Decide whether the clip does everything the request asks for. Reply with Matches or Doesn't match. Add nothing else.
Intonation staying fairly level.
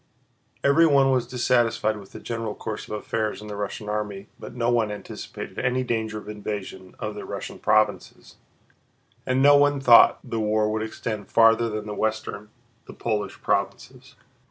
Matches